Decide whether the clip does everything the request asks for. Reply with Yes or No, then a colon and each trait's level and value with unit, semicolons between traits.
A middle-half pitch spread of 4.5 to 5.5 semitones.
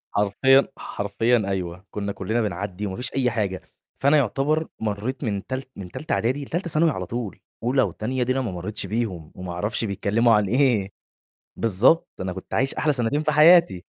Yes: average, 5.2 semitones